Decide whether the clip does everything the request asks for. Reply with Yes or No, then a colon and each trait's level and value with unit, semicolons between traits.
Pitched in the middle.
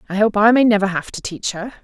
No: high, 205 Hz